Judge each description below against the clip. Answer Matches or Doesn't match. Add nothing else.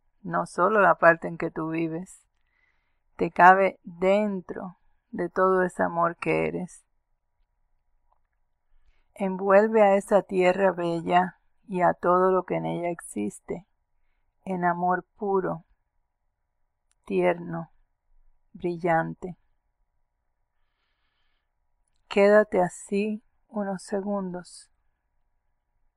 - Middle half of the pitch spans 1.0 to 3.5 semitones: Matches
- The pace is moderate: Doesn't match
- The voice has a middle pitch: Matches